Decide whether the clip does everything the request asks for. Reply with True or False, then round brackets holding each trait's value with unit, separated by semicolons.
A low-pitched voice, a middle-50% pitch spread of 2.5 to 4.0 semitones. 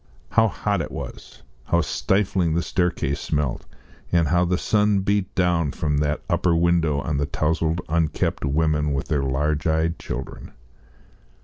True (80 Hz; 2.8 semitones)